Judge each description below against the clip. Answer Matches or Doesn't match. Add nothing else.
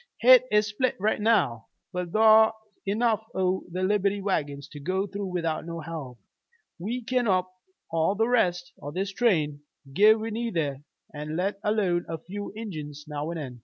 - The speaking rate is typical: Matches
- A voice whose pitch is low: Doesn't match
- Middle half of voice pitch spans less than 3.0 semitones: Doesn't match